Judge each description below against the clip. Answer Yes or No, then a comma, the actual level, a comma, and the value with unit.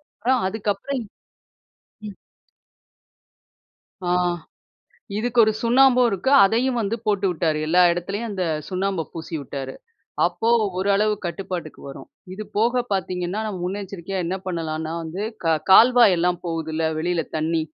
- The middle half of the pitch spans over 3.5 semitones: Yes, average, 4.5 semitones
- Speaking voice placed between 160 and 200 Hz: Yes, high, 190 Hz